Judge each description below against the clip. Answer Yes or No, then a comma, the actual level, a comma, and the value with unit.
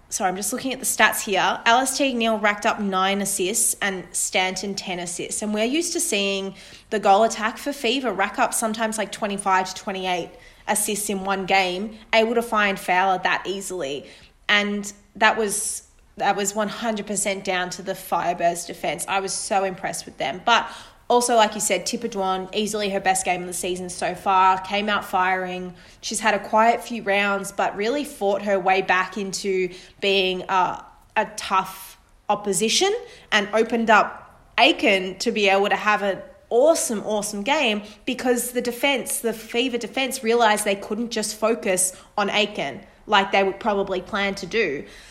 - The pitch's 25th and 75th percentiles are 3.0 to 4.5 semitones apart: No, narrow, 2.6 semitones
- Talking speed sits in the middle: Yes, average, 180 wpm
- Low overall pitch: No, high, 205 Hz